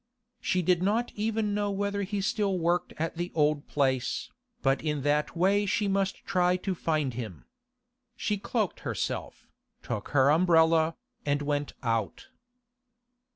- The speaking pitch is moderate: Yes, medium, 175 Hz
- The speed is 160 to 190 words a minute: No, average, 145 wpm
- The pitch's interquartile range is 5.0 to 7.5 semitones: Yes, average, 5.3 semitones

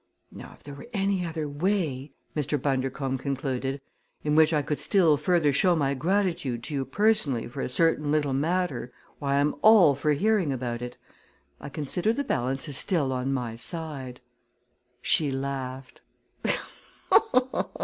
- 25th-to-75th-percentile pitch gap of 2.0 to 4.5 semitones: Yes, average, 3.8 semitones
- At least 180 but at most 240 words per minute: No, average, 150 wpm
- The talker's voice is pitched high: No, medium, 145 Hz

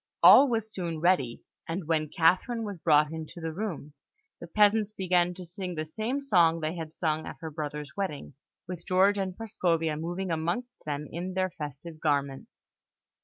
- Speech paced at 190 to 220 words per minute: No, average, 170 wpm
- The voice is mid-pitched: Yes, medium, 170 Hz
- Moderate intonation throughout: Yes, average, 3.6 semitones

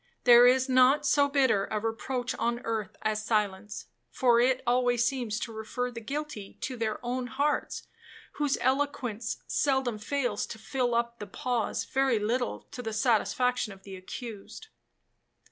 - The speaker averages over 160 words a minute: No, average, 155 wpm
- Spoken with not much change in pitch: No, average, 3.1 semitones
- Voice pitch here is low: No, high, 240 Hz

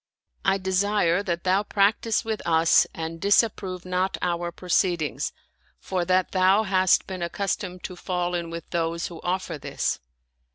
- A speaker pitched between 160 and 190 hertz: Yes, medium, 185 Hz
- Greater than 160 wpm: No, average, 155 wpm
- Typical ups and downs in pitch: No, narrow, 2.1 semitones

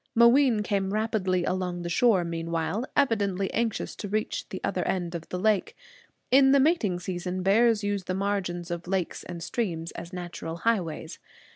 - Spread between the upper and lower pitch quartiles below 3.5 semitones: No, average, 3.8 semitones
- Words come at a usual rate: Yes, average, 165 wpm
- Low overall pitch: No, high, 190 Hz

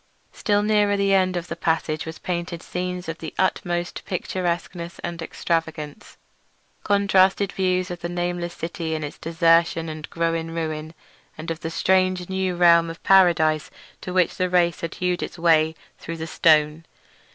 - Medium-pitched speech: Yes, medium, 170 Hz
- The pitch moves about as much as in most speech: No, narrow, 2.0 semitones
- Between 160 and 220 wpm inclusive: Yes, average, 165 wpm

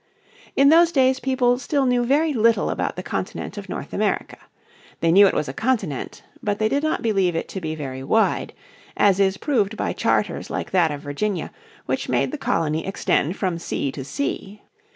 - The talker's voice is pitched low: No, high, 205 Hz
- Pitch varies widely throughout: Yes, wide, 7.7 semitones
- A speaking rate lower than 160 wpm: No, average, 195 wpm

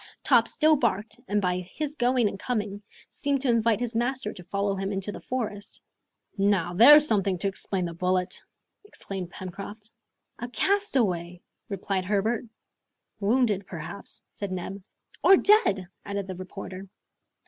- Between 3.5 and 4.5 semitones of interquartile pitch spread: Yes, average, 4.2 semitones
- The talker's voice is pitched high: Yes, high, 200 Hz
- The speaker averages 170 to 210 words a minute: No, average, 145 wpm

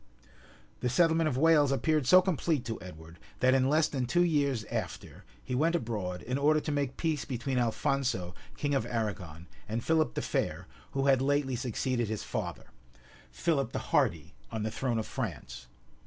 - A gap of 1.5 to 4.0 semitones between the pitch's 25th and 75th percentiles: No, average, 5.0 semitones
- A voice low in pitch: Yes, low, 130 Hz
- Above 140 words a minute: Yes, average, 180 wpm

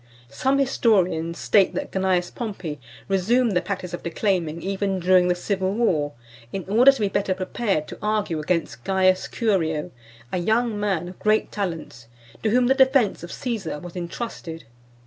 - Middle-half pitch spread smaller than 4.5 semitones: Yes, average, 3.9 semitones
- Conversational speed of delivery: Yes, average, 165 wpm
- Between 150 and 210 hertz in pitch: Yes, high, 190 Hz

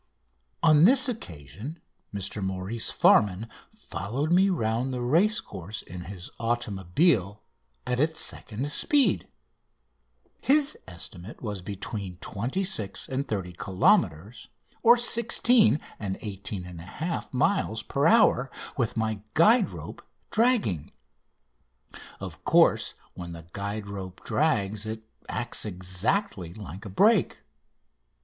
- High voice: No, low, 110 Hz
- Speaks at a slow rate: Yes, slow, 110 wpm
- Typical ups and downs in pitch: No, wide, 9.0 semitones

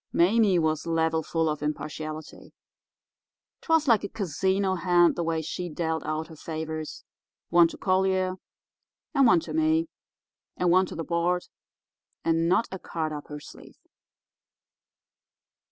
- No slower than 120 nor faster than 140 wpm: Yes, slow, 135 wpm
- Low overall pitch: No, medium, 170 Hz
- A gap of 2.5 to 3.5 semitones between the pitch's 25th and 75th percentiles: Yes, average, 2.9 semitones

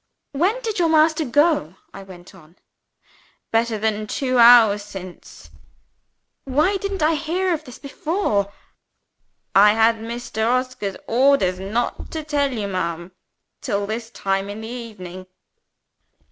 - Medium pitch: No, high, 230 Hz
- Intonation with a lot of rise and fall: Yes, wide, 6.6 semitones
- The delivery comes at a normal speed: No, slow, 130 wpm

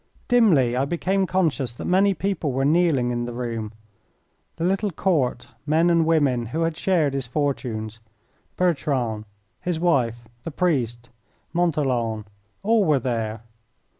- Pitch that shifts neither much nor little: No, wide, 6.4 semitones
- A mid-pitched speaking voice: Yes, medium, 145 Hz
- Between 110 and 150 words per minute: Yes, slow, 135 wpm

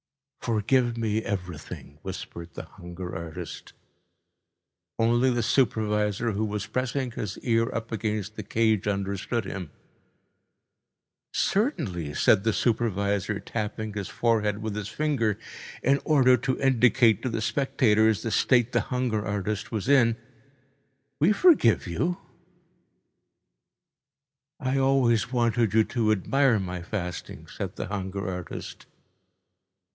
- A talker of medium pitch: No, low, 110 Hz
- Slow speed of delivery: Yes, slow, 120 wpm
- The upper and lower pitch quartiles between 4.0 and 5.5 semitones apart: No, average, 3.6 semitones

